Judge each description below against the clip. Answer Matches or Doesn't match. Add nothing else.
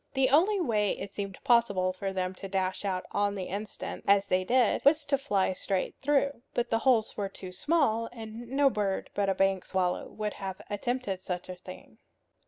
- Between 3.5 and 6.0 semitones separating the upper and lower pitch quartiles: Matches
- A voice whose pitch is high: Matches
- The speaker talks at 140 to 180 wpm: Doesn't match